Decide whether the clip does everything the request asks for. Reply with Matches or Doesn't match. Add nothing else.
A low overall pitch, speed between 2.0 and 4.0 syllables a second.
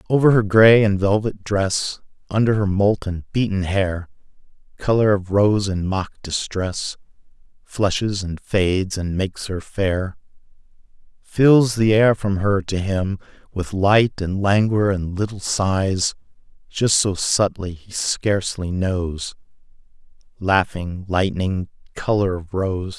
Matches